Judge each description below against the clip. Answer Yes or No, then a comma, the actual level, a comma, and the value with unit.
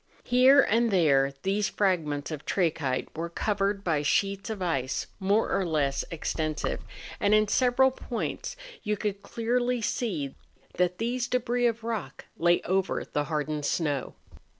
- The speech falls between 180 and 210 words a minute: No, average, 145 wpm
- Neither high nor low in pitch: No, high, 195 Hz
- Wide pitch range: Yes, wide, 6.6 semitones